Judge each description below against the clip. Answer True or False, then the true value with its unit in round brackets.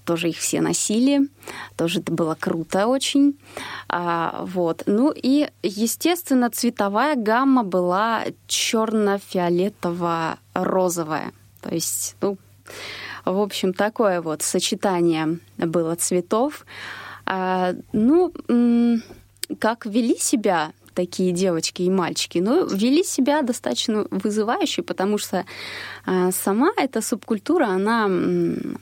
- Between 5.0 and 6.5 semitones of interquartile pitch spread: True (5.6 semitones)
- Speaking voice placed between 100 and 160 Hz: False (205 Hz)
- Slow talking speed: True (100 wpm)